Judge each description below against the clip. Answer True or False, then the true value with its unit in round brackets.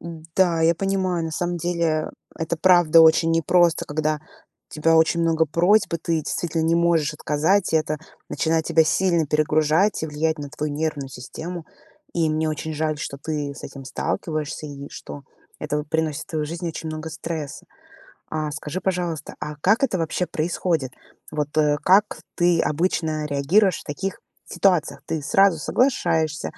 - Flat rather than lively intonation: True (2.1 semitones)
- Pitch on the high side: False (160 Hz)